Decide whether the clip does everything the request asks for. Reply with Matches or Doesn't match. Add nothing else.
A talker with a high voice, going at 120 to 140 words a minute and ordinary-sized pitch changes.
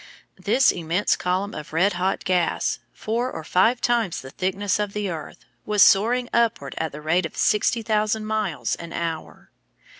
Doesn't match